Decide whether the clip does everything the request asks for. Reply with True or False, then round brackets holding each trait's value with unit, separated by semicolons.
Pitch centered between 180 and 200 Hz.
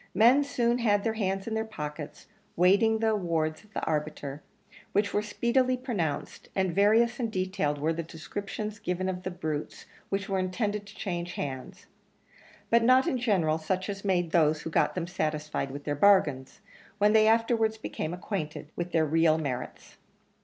True (190 Hz)